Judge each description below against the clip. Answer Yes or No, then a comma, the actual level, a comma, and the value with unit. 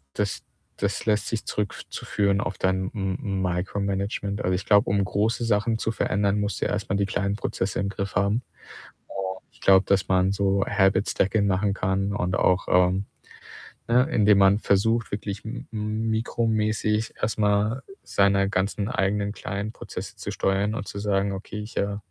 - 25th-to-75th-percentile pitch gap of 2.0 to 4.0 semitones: No, narrow, 1.6 semitones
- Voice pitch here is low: Yes, low, 100 Hz